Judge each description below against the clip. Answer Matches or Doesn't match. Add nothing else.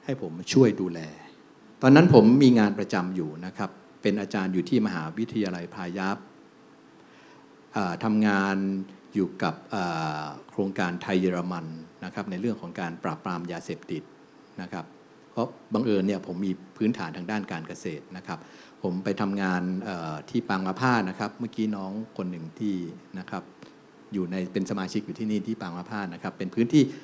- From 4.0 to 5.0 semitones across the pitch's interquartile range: Doesn't match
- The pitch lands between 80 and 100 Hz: Matches